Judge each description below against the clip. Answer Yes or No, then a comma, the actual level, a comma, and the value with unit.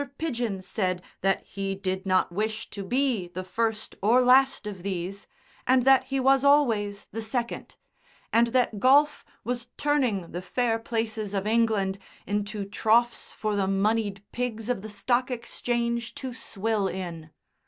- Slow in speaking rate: No, average, 155 wpm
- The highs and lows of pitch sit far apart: No, average, 3.9 semitones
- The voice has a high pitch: Yes, high, 220 Hz